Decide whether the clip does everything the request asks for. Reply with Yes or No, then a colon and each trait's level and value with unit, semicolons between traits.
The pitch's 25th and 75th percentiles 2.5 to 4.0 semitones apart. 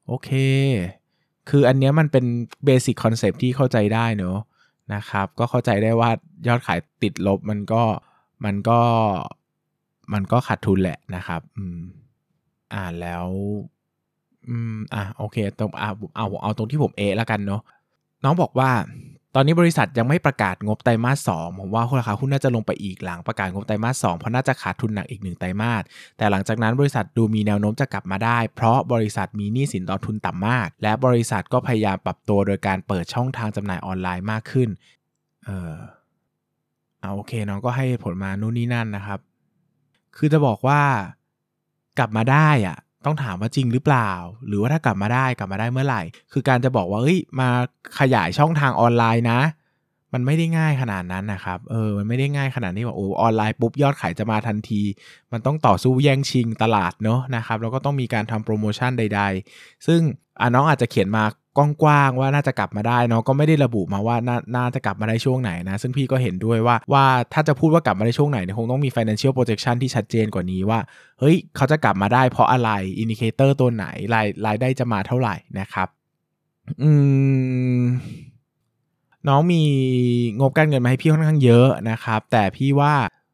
No: average, 4.4 semitones